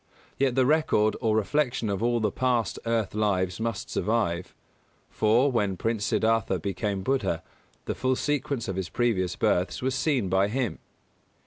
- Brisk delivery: No, average, 155 wpm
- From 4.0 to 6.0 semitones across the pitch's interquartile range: Yes, average, 4.5 semitones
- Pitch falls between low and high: No, low, 110 Hz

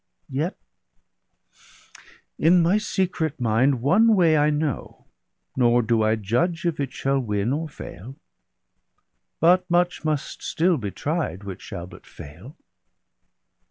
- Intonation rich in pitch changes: Yes, wide, 6.7 semitones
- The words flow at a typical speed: No, slow, 125 wpm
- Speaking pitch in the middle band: Yes, medium, 145 Hz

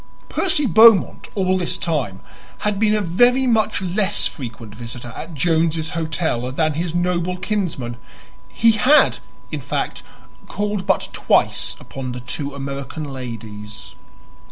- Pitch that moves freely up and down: Yes, wide, 7.6 semitones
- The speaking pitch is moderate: Yes, medium, 165 Hz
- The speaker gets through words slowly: Yes, slow, 130 wpm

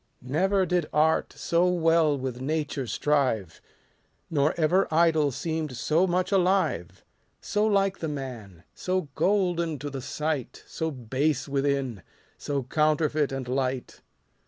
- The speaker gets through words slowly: Yes, slow, 130 wpm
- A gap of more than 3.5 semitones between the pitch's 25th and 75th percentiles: Yes, average, 4.1 semitones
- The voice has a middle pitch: Yes, medium, 150 Hz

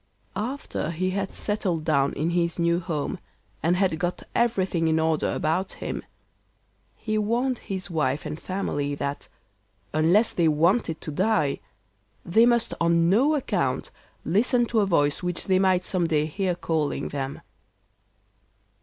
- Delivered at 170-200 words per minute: No, average, 145 wpm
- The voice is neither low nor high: Yes, medium, 175 Hz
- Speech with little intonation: No, average, 4.1 semitones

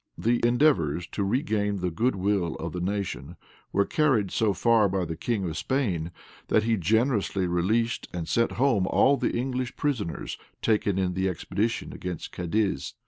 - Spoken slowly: No, average, 165 wpm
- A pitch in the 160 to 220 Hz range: No, low, 100 Hz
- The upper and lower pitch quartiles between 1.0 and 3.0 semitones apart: No, average, 4.7 semitones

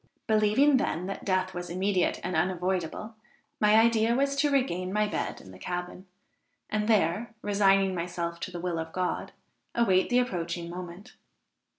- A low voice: No, medium, 185 Hz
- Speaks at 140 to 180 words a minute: Yes, average, 160 wpm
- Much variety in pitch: No, average, 3.4 semitones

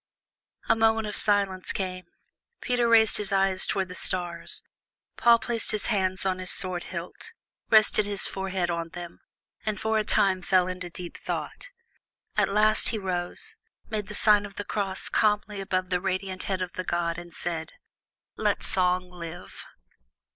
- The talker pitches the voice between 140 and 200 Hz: Yes, high, 190 Hz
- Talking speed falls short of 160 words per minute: No, average, 165 wpm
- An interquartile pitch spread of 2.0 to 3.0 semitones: Yes, narrow, 2.6 semitones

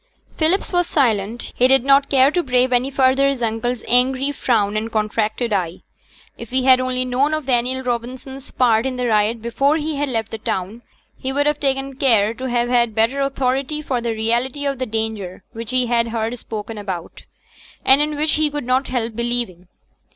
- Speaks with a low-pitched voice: No, very high, 250 Hz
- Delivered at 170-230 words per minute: Yes, average, 195 wpm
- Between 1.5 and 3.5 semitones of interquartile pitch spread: Yes, average, 3.2 semitones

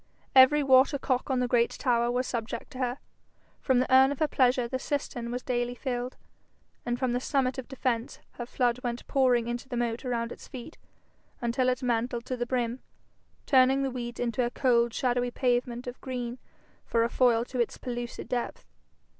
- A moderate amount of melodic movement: No, narrow, 1.4 semitones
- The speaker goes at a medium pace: Yes, average, 190 wpm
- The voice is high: Yes, high, 245 Hz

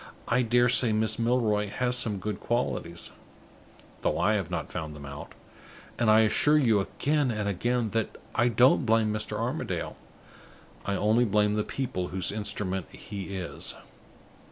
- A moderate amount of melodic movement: Yes, average, 3.3 semitones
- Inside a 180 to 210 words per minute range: No, average, 155 wpm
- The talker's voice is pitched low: Yes, low, 110 Hz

